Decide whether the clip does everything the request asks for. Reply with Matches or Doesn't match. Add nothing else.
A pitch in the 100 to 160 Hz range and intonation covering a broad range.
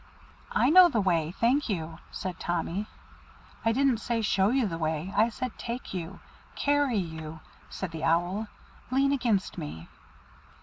Doesn't match